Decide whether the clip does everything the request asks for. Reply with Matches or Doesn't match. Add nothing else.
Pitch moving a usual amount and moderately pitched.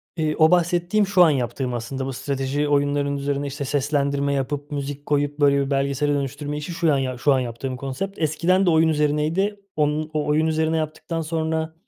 Doesn't match